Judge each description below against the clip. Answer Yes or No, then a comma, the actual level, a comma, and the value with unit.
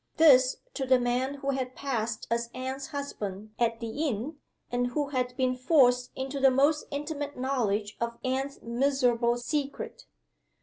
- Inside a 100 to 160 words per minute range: Yes, average, 150 wpm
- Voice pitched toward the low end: No, very high, 255 Hz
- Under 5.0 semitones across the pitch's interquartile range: Yes, narrow, 2.5 semitones